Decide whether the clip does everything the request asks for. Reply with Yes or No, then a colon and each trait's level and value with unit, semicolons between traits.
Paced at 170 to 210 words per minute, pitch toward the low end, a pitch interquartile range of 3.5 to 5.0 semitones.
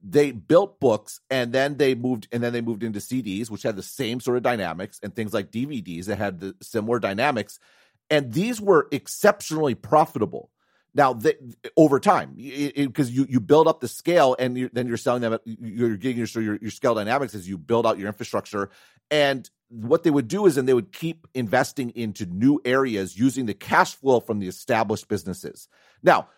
Yes: average, 200 wpm; low, 125 Hz; average, 3.9 semitones